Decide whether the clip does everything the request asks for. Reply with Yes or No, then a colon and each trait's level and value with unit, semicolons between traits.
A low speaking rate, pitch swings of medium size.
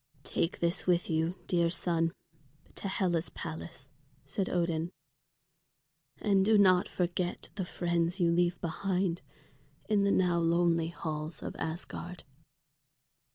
No: slow, 120 wpm; narrow, 1.6 semitones